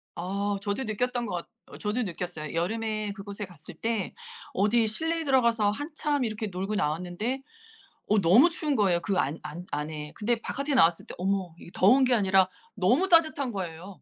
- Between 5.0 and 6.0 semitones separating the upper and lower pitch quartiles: Yes, average, 5.3 semitones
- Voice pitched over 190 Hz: Yes, high, 205 Hz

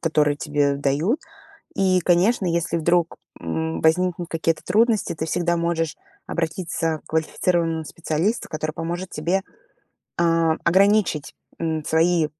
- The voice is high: No, medium, 165 Hz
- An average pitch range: No, narrow, 1.9 semitones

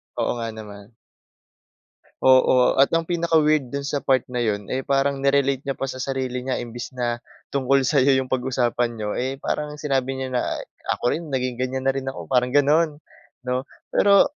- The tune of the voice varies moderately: No, narrow, 1.9 semitones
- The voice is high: No, low, 130 Hz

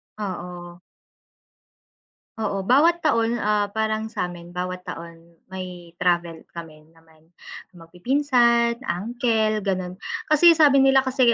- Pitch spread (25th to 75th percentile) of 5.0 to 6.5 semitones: Yes, wide, 5.4 semitones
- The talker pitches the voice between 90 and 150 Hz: No, high, 195 Hz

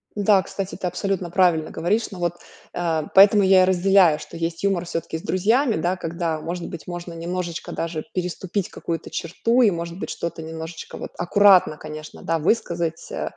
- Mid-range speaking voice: Yes, medium, 175 Hz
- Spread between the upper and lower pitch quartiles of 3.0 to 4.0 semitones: No, narrow, 2.5 semitones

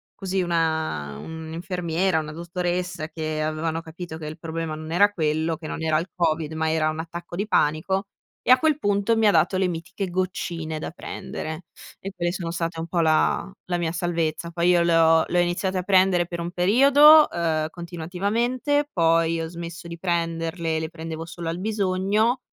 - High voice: No, medium, 170 Hz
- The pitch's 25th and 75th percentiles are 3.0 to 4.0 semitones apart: No, narrow, 2.4 semitones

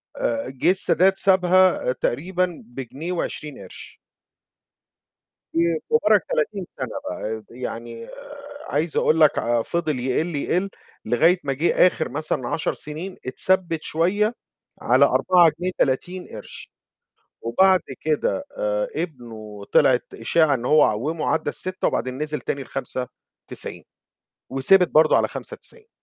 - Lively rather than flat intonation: Yes, wide, 6.3 semitones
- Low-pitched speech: No, medium, 160 Hz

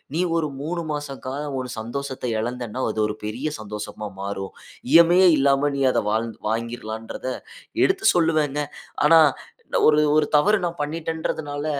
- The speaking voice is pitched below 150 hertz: Yes, medium, 140 Hz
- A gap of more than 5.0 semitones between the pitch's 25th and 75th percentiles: Yes, wide, 5.4 semitones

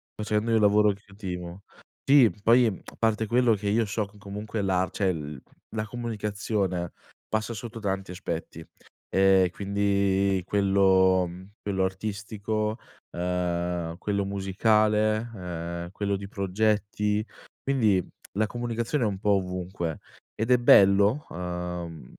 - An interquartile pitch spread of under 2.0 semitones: No, narrow, 2.6 semitones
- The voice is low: Yes, low, 100 Hz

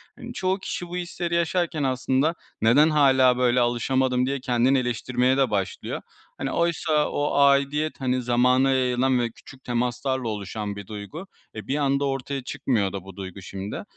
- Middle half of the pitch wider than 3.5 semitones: No, average, 2.8 semitones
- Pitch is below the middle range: Yes, low, 130 Hz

